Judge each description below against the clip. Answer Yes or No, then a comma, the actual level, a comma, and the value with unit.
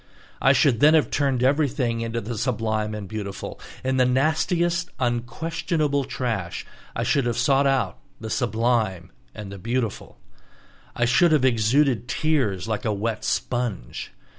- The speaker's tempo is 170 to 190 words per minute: No, average, 150 wpm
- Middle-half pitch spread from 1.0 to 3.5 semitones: No, average, 4.3 semitones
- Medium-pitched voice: No, low, 120 Hz